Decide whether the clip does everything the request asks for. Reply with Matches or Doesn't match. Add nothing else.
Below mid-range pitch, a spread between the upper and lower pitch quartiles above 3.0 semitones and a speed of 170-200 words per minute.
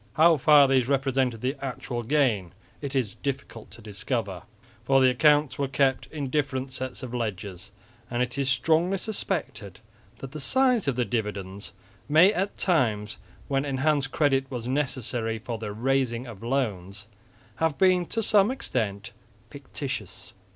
Doesn't match